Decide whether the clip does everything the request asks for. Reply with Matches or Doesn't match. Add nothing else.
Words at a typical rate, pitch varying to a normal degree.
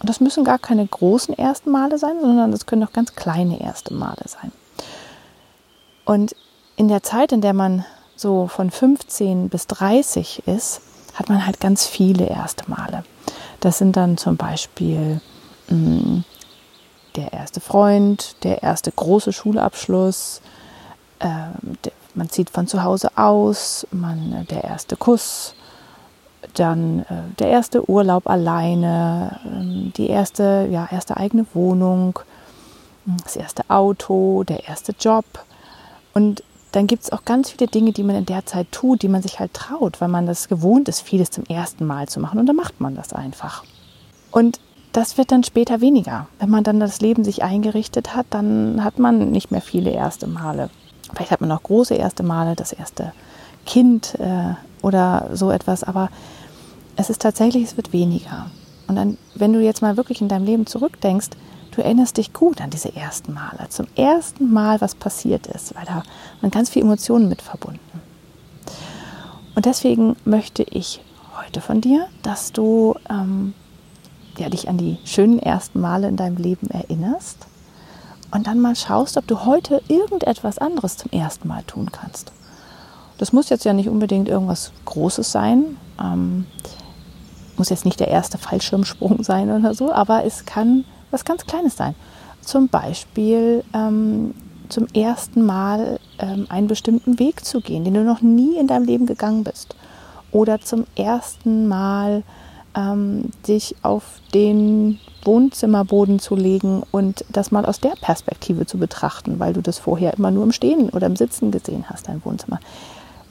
Matches